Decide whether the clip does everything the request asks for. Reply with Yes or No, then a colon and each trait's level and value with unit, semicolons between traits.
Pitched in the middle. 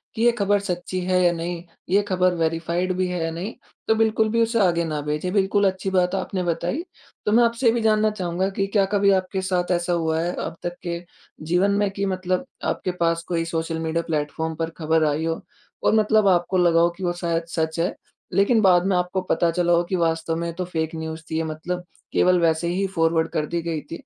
Yes: medium, 175 Hz